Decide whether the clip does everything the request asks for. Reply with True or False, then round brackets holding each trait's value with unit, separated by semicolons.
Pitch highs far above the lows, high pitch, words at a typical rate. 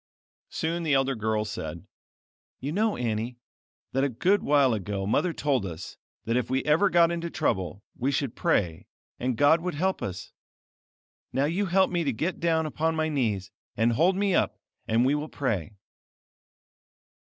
False (7.0 semitones; 140 Hz; 170 wpm)